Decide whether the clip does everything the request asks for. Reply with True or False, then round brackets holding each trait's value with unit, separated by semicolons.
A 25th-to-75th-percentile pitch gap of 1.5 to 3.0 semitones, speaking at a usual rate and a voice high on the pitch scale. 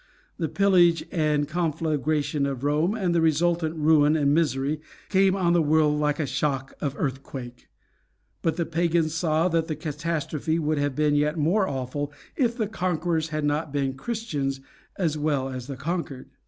False (2.7 semitones; 165 wpm; 155 Hz)